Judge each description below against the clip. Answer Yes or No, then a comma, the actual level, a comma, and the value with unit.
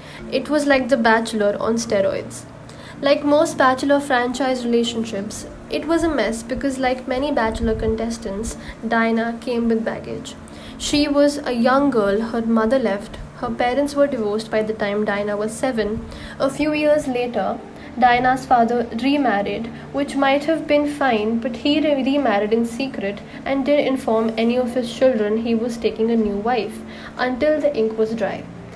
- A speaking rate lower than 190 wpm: Yes, average, 165 wpm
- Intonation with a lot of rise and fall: No, average, 3.7 semitones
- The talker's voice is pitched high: Yes, high, 245 Hz